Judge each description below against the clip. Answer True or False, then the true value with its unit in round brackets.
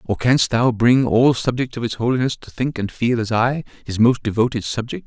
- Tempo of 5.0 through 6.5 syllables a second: True (5.3 syllables/s)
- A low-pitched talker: True (120 Hz)